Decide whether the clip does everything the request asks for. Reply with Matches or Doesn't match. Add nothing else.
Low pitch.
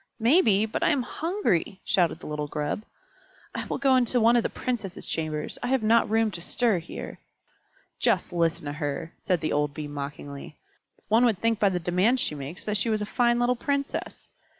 Doesn't match